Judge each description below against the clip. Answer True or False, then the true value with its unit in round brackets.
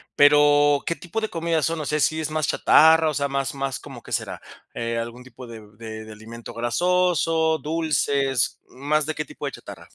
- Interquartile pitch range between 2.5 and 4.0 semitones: False (4.9 semitones)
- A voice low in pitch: False (145 Hz)